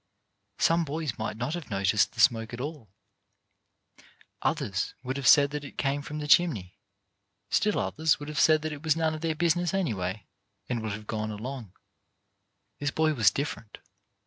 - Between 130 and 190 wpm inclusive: Yes, average, 175 wpm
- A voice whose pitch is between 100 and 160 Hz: Yes, medium, 140 Hz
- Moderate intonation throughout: No, wide, 6.1 semitones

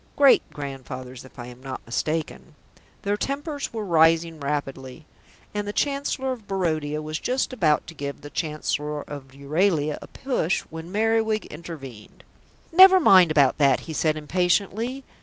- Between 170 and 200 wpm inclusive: No, average, 150 wpm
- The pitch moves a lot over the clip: Yes, wide, 6.5 semitones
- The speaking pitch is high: No, medium, 160 Hz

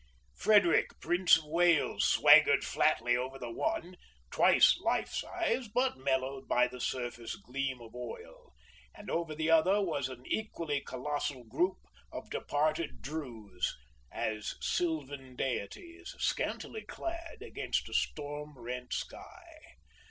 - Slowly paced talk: Yes, slow, 125 wpm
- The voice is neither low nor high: Yes, medium, 145 Hz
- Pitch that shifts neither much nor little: No, wide, 5.8 semitones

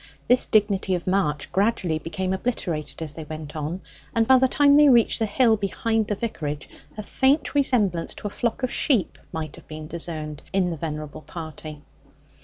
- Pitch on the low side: No, high, 190 Hz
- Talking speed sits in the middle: Yes, average, 185 wpm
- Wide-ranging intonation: Yes, wide, 6.5 semitones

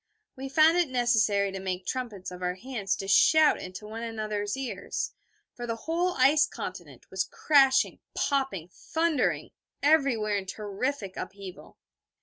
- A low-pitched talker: No, high, 230 Hz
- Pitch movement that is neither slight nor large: No, wide, 5.8 semitones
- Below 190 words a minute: Yes, average, 140 wpm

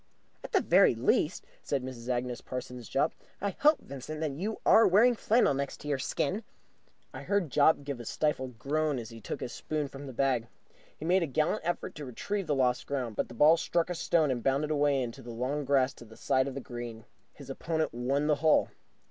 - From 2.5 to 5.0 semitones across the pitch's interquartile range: Yes, average, 3.8 semitones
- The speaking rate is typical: No, fast, 215 wpm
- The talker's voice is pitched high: No, medium, 140 Hz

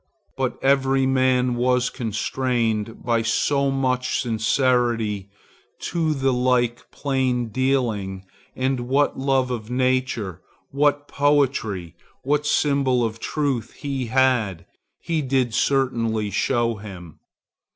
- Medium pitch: No, low, 125 Hz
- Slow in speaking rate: Yes, slow, 105 wpm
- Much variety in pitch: No, average, 2.9 semitones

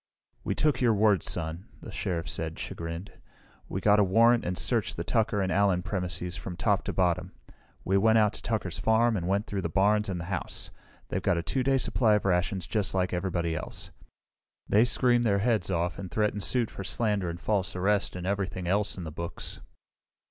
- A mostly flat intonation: No, average, 3.3 semitones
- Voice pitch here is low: Yes, very low, 95 Hz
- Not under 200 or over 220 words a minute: Yes, fast, 205 wpm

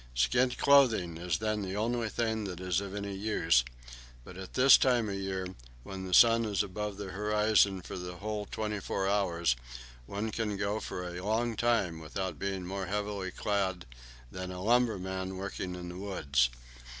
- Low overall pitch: Yes, low, 100 Hz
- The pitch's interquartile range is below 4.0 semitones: Yes, average, 2.7 semitones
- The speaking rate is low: No, average, 175 wpm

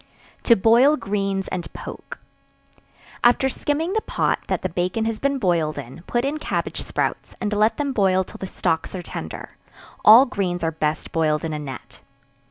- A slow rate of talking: No, average, 180 wpm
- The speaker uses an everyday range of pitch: No, wide, 6.3 semitones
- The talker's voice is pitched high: Yes, high, 195 Hz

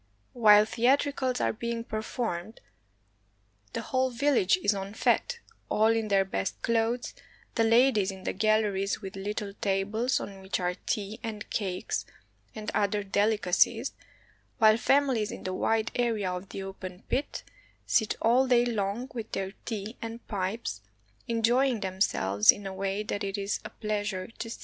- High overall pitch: Yes, high, 215 Hz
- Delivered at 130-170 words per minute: Yes, average, 160 wpm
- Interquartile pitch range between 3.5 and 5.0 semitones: No, average, 3.1 semitones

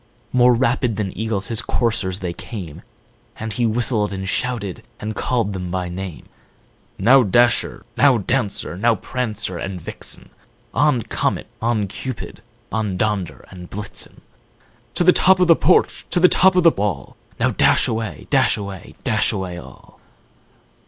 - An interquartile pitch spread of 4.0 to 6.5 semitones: Yes, average, 4.3 semitones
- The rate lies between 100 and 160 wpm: Yes, average, 155 wpm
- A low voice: Yes, low, 110 Hz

